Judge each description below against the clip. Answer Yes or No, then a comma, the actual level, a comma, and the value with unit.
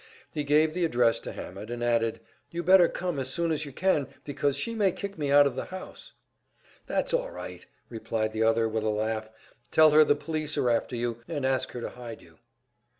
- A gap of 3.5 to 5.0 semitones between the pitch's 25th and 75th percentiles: No, wide, 5.5 semitones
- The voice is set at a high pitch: No, medium, 140 Hz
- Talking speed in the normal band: No, fast, 215 wpm